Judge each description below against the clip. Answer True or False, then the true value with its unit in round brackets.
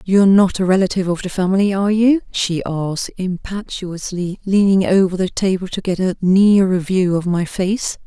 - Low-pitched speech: False (190 Hz)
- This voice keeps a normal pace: True (180 wpm)